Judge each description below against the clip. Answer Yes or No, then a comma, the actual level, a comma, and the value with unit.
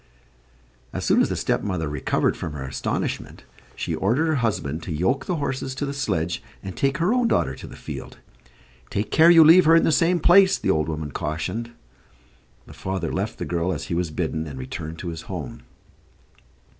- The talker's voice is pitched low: Yes, very low, 95 Hz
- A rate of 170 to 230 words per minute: Yes, average, 195 wpm